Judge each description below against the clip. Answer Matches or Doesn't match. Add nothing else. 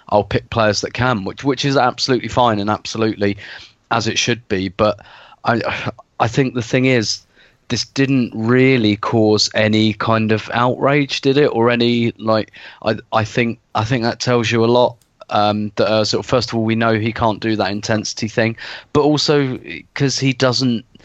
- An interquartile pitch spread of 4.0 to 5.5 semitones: Doesn't match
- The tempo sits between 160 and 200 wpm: Matches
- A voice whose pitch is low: Matches